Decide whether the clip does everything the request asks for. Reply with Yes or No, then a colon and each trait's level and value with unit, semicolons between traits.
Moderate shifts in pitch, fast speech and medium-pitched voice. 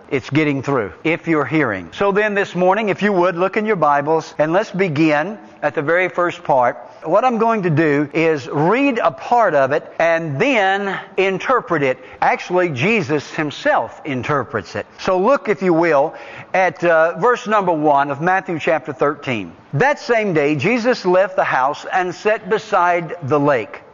No: average, 4.7 semitones; average, 180 wpm; medium, 175 Hz